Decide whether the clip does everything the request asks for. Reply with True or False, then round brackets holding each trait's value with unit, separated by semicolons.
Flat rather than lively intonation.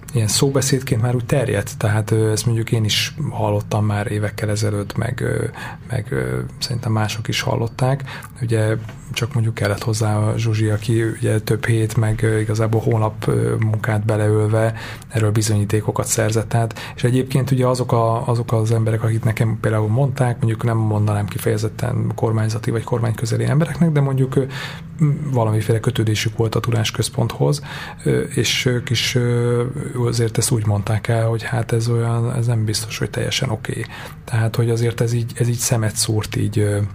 True (2.1 semitones)